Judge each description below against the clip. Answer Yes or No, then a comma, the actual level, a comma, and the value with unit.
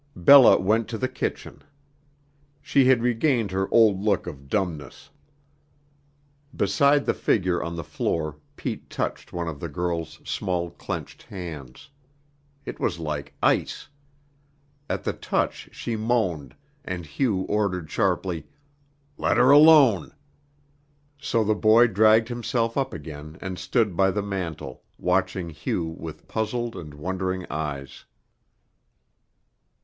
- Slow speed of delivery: Yes, slow, 125 wpm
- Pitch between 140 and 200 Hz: No, very low, 95 Hz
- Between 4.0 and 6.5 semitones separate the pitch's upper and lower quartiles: Yes, wide, 5.5 semitones